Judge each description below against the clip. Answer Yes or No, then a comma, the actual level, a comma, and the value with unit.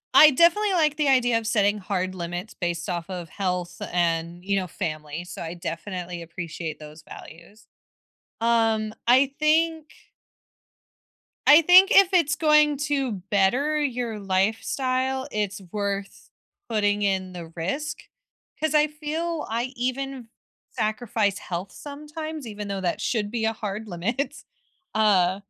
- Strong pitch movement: Yes, wide, 7.4 semitones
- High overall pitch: Yes, high, 215 Hz